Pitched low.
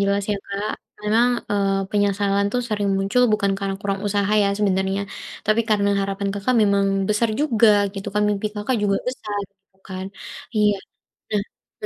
No: high, 200 Hz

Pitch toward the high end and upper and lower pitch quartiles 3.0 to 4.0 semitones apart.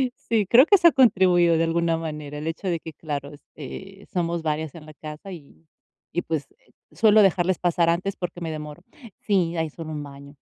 No: medium, 165 Hz; average, 3.4 semitones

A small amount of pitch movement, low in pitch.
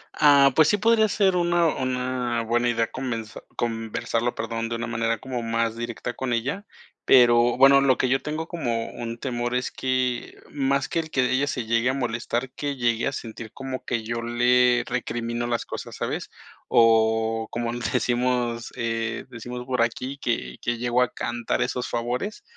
Yes: narrow, 2.1 semitones; low, 120 Hz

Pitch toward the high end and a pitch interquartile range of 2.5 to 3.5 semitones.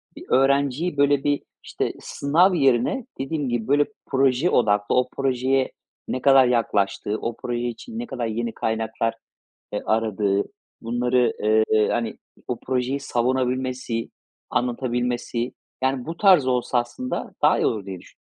No: low, 125 Hz; average, 2.9 semitones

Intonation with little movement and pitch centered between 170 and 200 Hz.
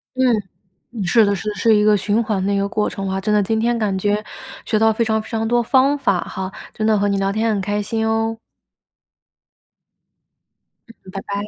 No: narrow, 1.9 semitones; high, 215 Hz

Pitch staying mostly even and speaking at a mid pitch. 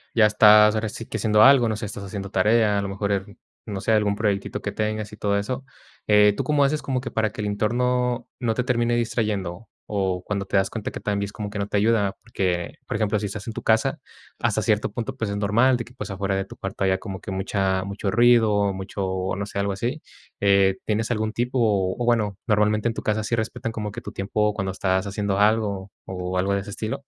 No: narrow, 2.3 semitones; low, 105 Hz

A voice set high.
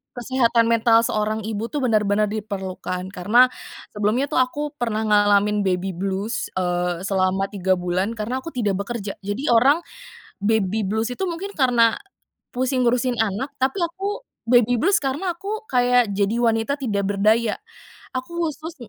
Yes: high, 225 Hz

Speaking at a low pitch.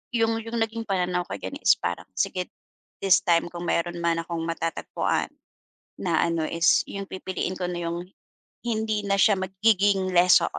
No: medium, 185 Hz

